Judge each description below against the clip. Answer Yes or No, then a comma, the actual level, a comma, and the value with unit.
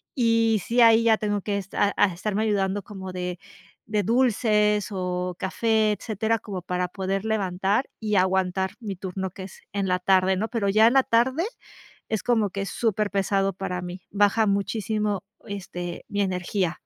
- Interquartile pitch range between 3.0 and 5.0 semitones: No, narrow, 2.5 semitones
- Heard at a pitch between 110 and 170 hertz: No, high, 200 Hz